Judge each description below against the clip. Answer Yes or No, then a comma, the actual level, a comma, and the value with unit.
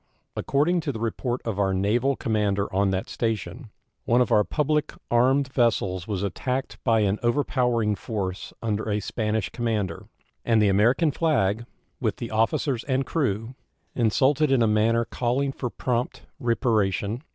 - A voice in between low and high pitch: No, low, 115 Hz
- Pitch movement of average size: Yes, average, 3.7 semitones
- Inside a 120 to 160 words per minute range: Yes, average, 155 wpm